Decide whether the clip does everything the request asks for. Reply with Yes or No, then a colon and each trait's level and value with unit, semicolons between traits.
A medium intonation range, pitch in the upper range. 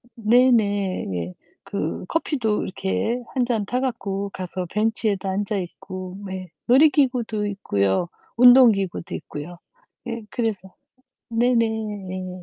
Yes: average, 4.2 semitones; high, 205 Hz